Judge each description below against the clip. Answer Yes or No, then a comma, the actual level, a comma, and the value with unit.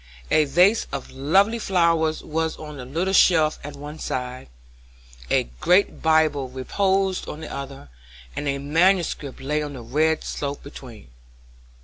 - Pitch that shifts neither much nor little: Yes, average, 3.4 semitones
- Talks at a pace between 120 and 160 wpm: Yes, average, 145 wpm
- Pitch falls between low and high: Yes, medium, 150 Hz